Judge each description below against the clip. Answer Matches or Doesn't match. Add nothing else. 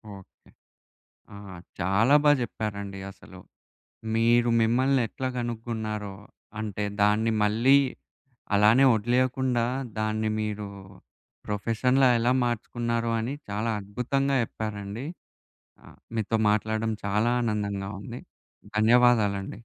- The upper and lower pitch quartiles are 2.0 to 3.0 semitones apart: Matches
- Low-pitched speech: Matches